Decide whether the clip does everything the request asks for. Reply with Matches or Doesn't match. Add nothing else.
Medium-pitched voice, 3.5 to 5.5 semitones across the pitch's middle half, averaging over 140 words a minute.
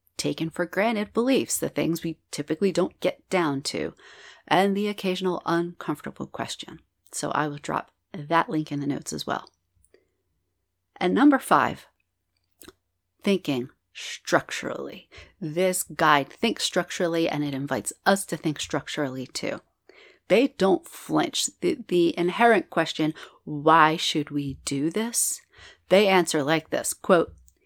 Doesn't match